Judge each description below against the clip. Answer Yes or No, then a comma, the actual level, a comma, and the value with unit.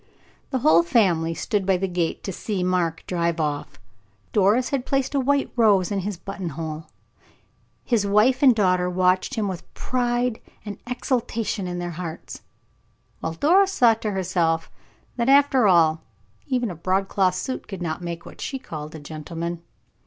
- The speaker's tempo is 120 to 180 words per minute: Yes, average, 160 wpm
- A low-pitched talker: No, high, 190 Hz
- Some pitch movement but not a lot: No, wide, 5.7 semitones